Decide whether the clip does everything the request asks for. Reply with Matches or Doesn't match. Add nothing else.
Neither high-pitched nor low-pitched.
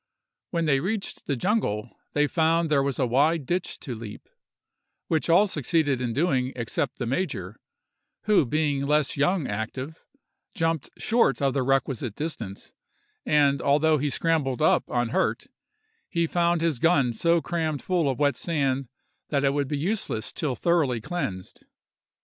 Matches